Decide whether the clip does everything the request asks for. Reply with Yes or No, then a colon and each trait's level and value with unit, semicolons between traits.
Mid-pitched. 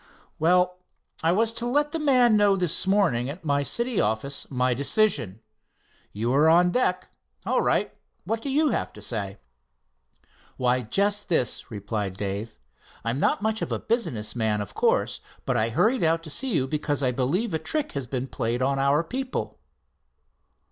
Yes: medium, 155 Hz